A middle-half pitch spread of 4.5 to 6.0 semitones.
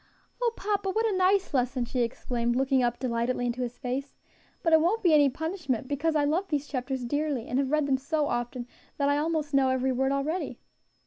No: average, 4.0 semitones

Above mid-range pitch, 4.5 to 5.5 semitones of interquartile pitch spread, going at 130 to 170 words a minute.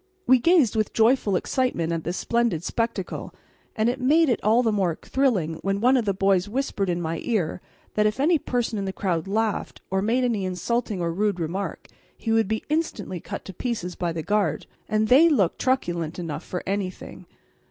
No: high, 210 Hz; average, 5.1 semitones; average, 195 wpm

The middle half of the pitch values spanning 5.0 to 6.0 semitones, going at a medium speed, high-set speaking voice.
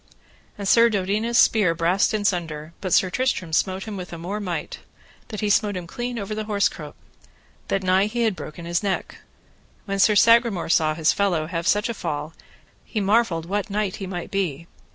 No: average, 3.7 semitones; average, 195 wpm; high, 195 Hz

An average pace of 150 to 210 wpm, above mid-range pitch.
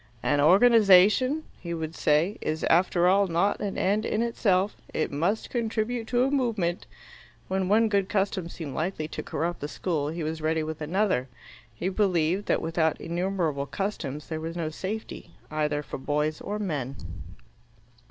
No: average, 160 wpm; medium, 175 Hz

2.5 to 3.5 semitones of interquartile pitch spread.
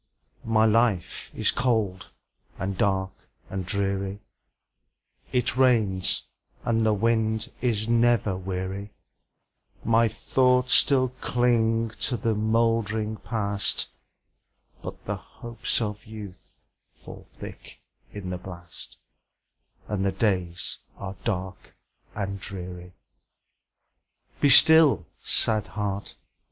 Yes: average, 3.1 semitones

